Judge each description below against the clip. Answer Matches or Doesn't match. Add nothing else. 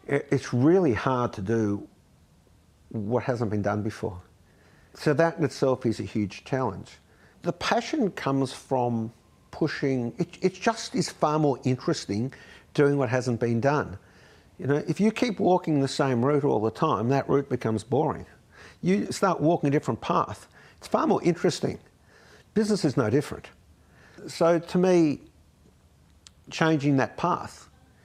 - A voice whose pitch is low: Matches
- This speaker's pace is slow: Doesn't match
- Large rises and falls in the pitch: Matches